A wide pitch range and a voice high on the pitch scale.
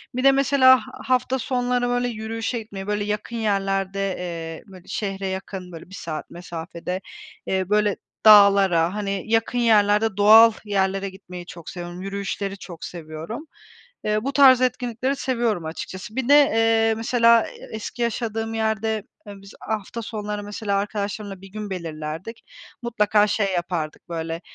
No: average, 3.1 semitones; high, 205 Hz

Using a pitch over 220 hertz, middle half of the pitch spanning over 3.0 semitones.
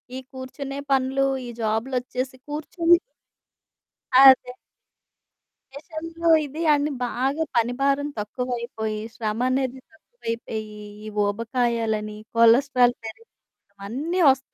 Yes: very high, 255 Hz; average, 3.5 semitones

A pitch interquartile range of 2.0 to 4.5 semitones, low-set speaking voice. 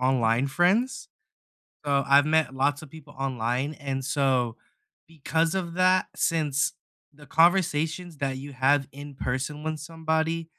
No: average, 3.2 semitones; medium, 145 Hz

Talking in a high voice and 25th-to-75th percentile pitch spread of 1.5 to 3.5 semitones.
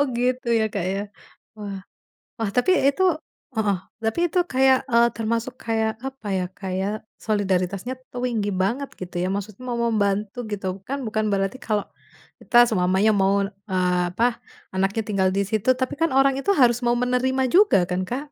No: high, 220 Hz; average, 4.1 semitones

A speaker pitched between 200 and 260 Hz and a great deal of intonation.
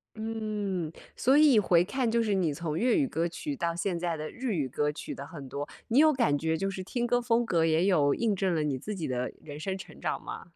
No: medium, 185 Hz; wide, 6.3 semitones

